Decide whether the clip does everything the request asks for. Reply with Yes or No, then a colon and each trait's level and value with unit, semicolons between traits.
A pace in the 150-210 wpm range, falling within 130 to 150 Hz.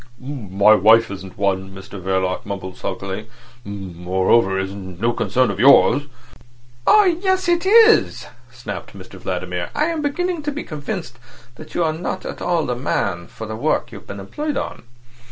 No: average, 165 wpm; low, 115 Hz